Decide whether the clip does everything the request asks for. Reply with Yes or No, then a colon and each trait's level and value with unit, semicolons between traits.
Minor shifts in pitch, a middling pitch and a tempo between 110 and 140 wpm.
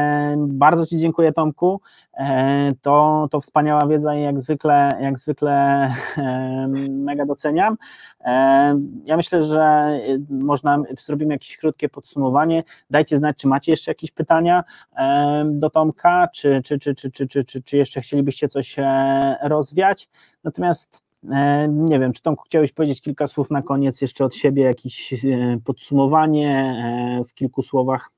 Yes: narrow, 2.0 semitones; medium, 145 Hz; average, 130 wpm